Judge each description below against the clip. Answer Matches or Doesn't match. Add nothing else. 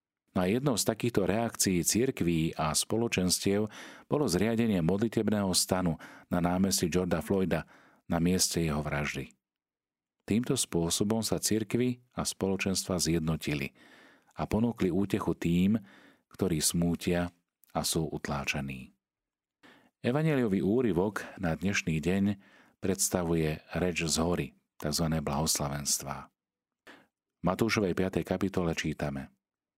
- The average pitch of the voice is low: Matches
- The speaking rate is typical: Doesn't match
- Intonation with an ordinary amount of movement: Matches